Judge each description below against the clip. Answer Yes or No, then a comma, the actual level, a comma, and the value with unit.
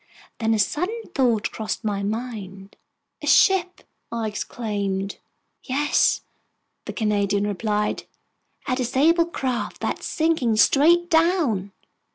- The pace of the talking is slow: Yes, slow, 110 wpm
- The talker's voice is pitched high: Yes, high, 230 Hz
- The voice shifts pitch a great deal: Yes, wide, 7.1 semitones